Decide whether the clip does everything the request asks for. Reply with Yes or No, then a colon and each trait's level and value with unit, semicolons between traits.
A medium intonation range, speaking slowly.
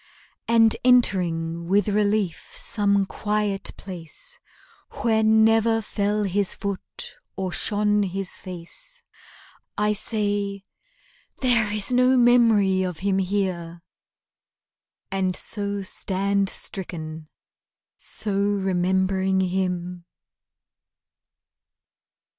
No: narrow, 2.2 semitones; slow, 85 wpm